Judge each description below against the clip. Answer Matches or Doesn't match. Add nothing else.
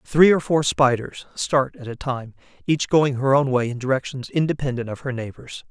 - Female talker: Doesn't match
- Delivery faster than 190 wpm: Matches